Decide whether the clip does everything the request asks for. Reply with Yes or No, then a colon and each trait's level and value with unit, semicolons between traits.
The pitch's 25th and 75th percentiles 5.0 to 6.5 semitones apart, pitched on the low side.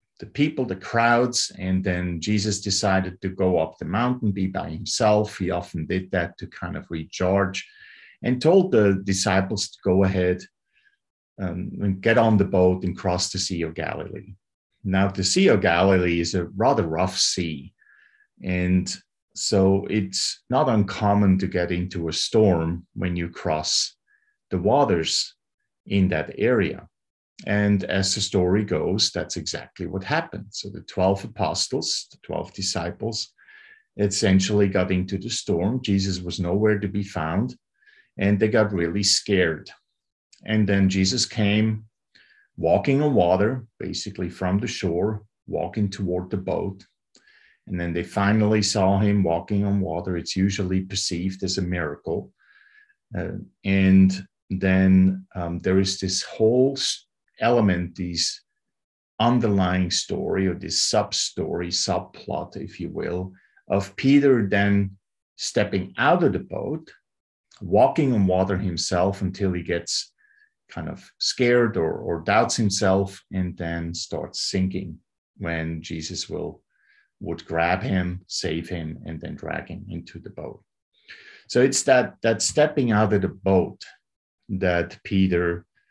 No: average, 2.9 semitones; very low, 95 Hz